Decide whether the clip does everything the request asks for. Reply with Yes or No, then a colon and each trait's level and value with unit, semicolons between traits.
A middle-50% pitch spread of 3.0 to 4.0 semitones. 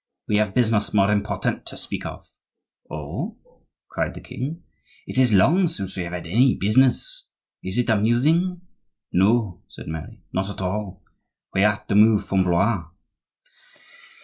No: average, 4.4 semitones